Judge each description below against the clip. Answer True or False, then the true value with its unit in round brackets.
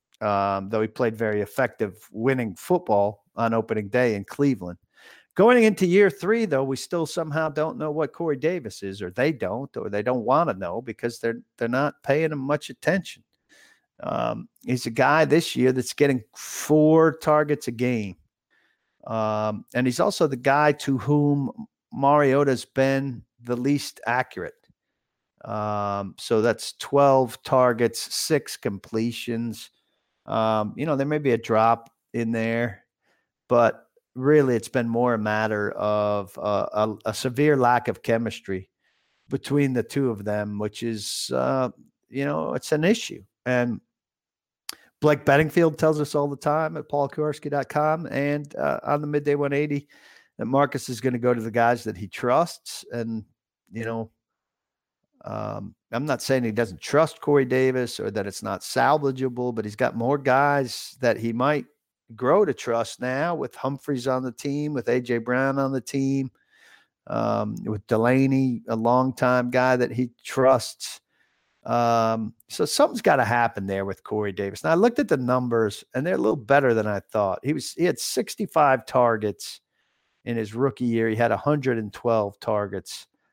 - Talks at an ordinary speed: True (165 wpm)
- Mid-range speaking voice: False (125 Hz)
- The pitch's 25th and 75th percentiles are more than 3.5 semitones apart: True (4.2 semitones)